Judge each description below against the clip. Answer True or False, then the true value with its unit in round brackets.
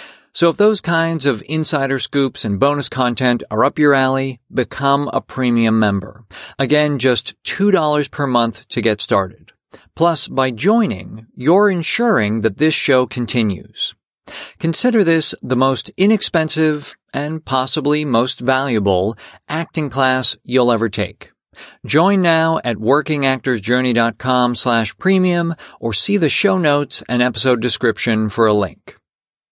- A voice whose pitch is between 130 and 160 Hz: True (135 Hz)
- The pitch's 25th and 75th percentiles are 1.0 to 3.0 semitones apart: False (5.2 semitones)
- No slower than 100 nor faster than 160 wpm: True (135 wpm)